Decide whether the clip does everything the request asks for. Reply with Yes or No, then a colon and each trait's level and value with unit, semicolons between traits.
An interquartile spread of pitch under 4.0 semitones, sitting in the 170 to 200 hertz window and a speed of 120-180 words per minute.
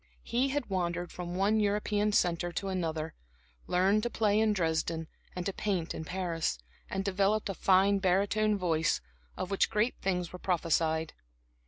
Yes: average, 3.1 semitones; high, 190 Hz; average, 160 wpm